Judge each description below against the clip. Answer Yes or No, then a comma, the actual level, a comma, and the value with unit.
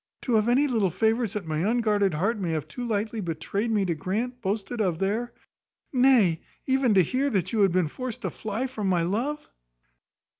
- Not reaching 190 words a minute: No, average, 195 wpm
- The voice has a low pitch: No, high, 215 Hz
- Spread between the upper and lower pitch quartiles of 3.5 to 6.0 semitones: Yes, average, 4.4 semitones